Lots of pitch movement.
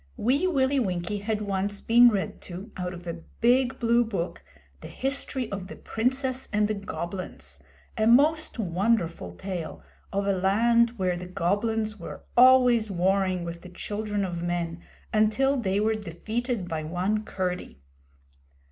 No: average, 4.6 semitones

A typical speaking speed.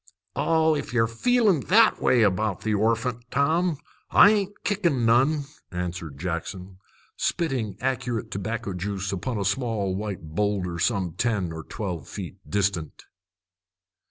No: slow, 130 wpm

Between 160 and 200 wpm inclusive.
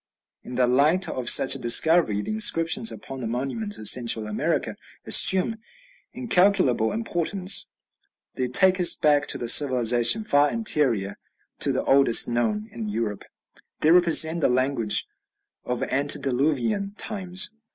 No: slow, 135 wpm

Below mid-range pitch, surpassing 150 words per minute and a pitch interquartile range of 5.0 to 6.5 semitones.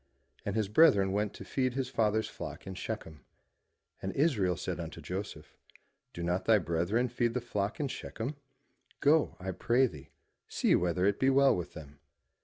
Yes: low, 105 Hz; average, 175 wpm; wide, 5.6 semitones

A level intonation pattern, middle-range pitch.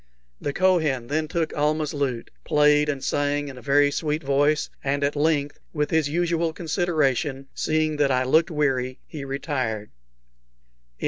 Yes: narrow, 2.2 semitones; medium, 145 Hz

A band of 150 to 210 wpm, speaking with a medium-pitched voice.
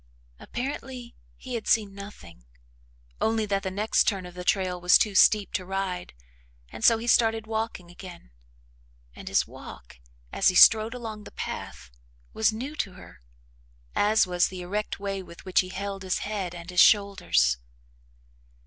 No: average, 165 wpm; high, 200 Hz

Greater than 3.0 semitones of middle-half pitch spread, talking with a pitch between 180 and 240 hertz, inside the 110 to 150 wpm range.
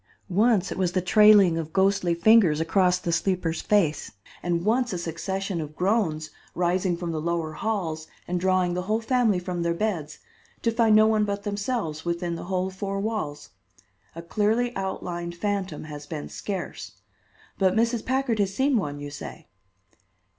No: average, 3.8 semitones; medium, 185 Hz; average, 170 wpm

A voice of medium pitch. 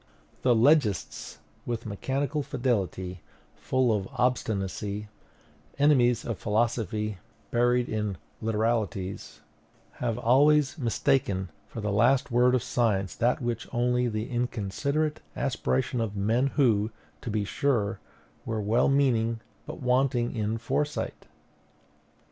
No: low, 120 Hz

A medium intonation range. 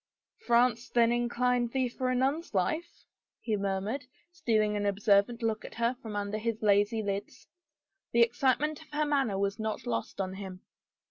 Yes: average, 3.6 semitones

